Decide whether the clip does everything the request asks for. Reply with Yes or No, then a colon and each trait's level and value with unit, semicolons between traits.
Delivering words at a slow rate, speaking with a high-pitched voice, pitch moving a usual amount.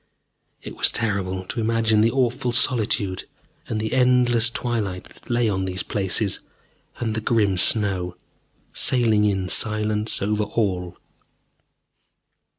No: slow, 125 wpm; low, 110 Hz; average, 3.2 semitones